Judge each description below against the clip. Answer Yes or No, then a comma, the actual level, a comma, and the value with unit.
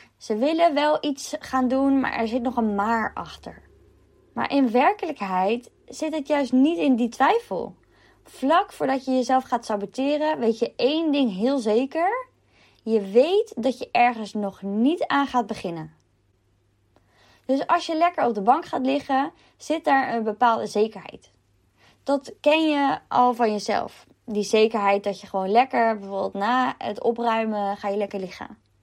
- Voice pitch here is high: Yes, high, 245 Hz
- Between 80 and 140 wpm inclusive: No, average, 165 wpm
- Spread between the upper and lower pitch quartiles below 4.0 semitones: No, wide, 5.5 semitones